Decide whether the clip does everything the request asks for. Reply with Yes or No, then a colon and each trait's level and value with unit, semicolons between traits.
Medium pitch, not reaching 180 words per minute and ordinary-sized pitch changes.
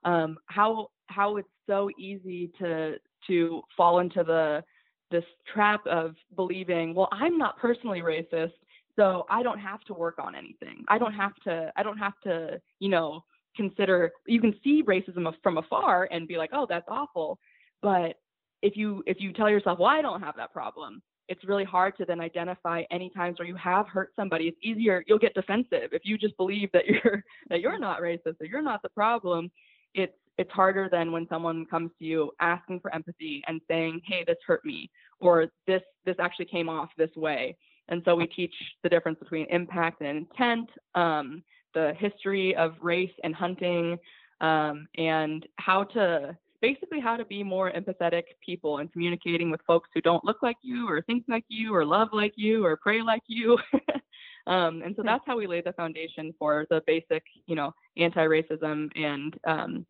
No: medium, 180 Hz; average, 190 wpm; average, 3.9 semitones